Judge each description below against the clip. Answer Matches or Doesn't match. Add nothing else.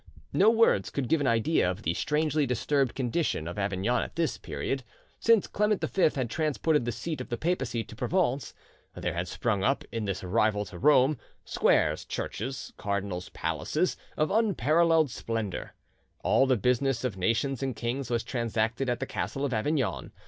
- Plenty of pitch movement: Matches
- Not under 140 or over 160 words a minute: Doesn't match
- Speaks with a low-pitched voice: Matches